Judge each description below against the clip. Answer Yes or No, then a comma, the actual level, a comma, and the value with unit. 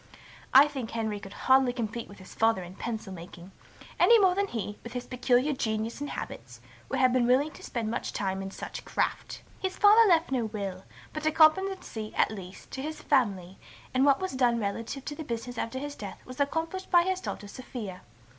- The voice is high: Yes, high, 245 Hz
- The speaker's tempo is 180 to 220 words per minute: Yes, fast, 205 wpm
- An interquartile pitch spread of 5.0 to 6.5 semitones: Yes, wide, 5.6 semitones